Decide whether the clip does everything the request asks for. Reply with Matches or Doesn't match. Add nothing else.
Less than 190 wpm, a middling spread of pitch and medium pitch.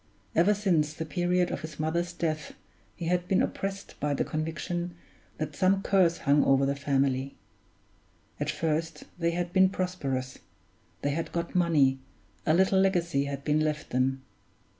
Matches